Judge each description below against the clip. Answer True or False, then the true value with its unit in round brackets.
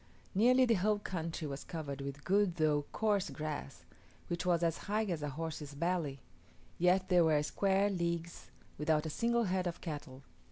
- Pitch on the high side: False (170 Hz)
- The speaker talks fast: False (170 wpm)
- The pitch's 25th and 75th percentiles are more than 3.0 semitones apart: True (4.2 semitones)